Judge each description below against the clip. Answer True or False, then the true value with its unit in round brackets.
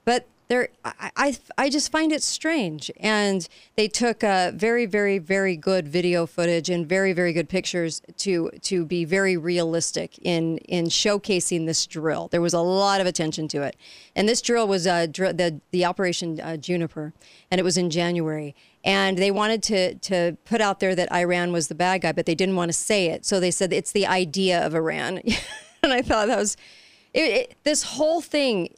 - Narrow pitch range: False (3.4 semitones)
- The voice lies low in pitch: False (185 Hz)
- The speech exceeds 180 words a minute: True (200 wpm)